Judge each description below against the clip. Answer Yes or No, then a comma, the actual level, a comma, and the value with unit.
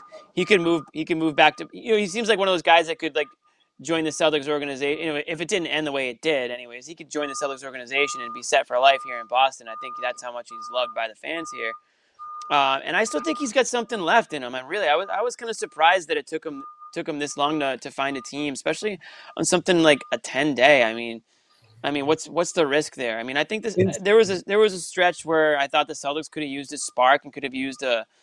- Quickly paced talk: Yes, fast, 290 wpm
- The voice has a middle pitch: Yes, medium, 160 Hz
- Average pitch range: No, wide, 7.3 semitones